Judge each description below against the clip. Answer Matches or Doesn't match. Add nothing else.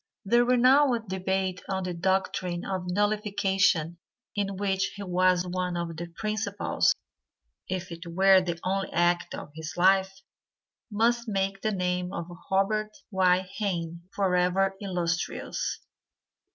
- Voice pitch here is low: Doesn't match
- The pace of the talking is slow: Matches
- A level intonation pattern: Matches